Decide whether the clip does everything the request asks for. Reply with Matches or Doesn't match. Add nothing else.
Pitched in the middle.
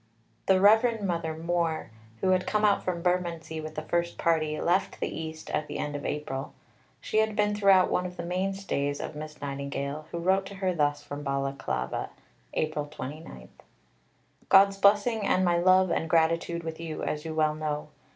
Matches